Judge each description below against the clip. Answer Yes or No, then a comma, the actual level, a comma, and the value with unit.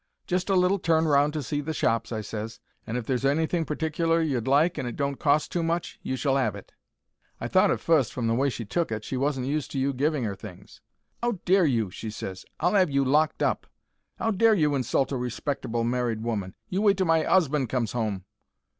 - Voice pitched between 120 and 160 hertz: Yes, medium, 140 Hz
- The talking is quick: Yes, fast, 225 wpm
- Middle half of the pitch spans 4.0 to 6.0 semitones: Yes, wide, 5.6 semitones